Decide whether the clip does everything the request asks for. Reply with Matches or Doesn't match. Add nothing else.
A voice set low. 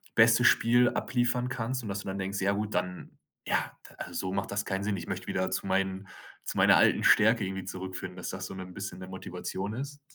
Matches